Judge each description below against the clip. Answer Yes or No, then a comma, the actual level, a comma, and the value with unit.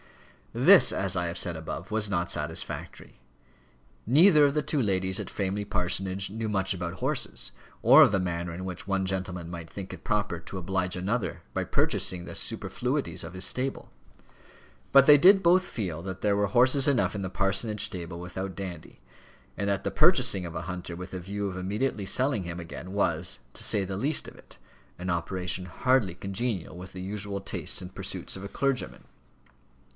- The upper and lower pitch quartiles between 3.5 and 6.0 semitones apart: No, average, 2.7 semitones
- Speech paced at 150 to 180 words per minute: No, average, 190 wpm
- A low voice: Yes, very low, 95 Hz